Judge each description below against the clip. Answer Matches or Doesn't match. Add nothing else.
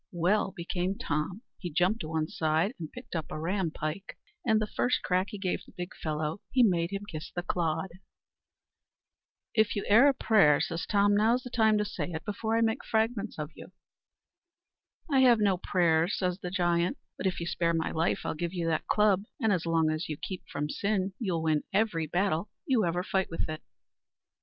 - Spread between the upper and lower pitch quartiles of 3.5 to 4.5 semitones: Matches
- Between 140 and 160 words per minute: Doesn't match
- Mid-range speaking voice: Matches